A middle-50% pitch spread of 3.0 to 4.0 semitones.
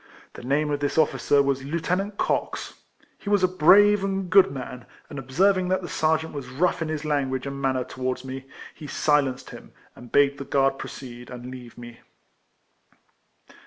No: average, 4.8 semitones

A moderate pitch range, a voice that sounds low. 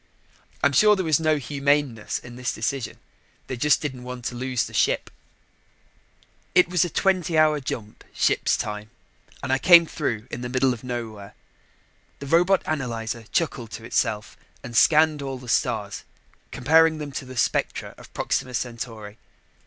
Yes: average, 4.7 semitones; low, 130 Hz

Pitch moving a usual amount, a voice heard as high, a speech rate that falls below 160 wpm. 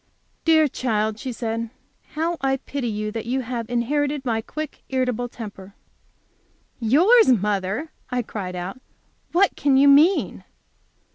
Yes: average, 4.6 semitones; high, 245 Hz; slow, 135 wpm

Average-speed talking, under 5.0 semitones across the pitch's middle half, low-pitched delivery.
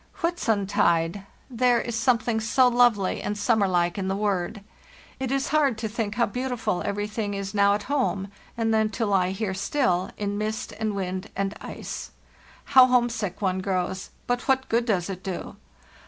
No: average, 175 wpm; average, 3.7 semitones; high, 210 Hz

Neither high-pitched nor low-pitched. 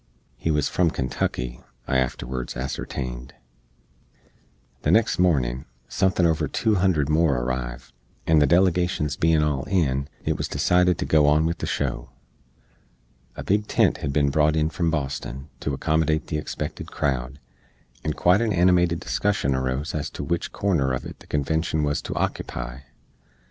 No: very low, 75 Hz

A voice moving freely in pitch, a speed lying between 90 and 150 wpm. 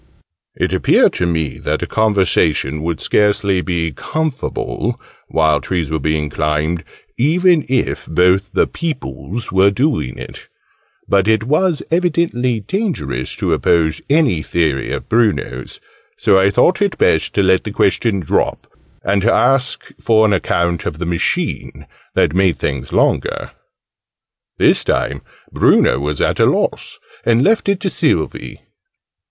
Yes: wide, 7.8 semitones; average, 145 wpm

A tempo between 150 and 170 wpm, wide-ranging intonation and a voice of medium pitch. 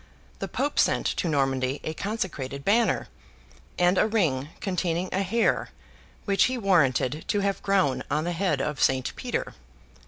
Yes: average, 155 wpm; wide, 6.1 semitones; medium, 175 Hz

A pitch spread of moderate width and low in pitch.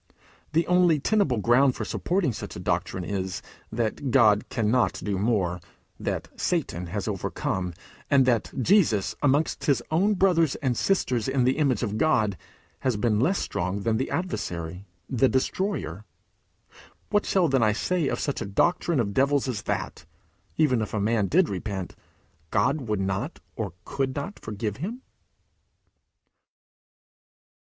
No: wide, 6.7 semitones; low, 125 Hz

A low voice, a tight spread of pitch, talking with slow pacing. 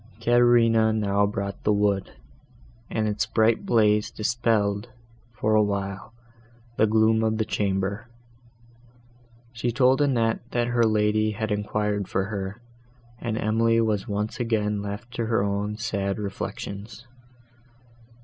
Yes: low, 110 Hz; narrow, 1.9 semitones; slow, 130 wpm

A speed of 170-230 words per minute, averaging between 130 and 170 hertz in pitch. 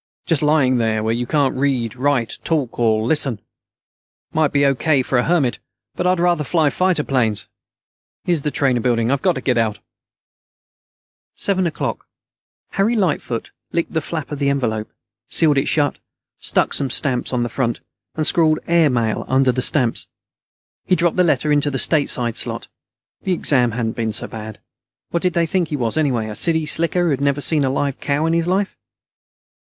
Yes: average, 190 wpm; medium, 140 Hz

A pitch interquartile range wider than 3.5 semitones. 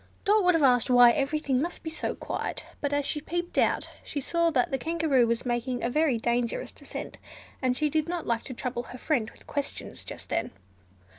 Yes: average, 4.4 semitones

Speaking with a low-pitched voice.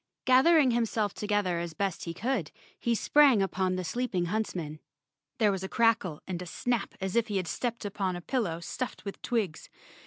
No: high, 205 Hz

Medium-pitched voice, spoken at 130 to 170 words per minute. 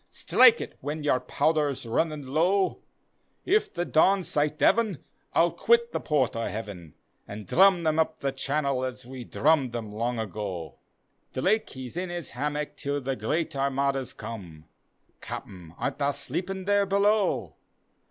Yes: medium, 145 Hz; average, 150 wpm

